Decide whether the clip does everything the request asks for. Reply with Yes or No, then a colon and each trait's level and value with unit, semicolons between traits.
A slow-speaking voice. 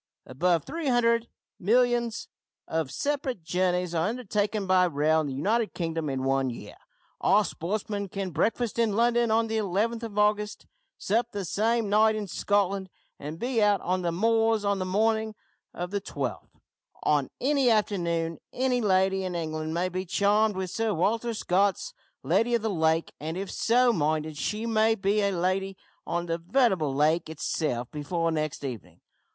No: average, 170 wpm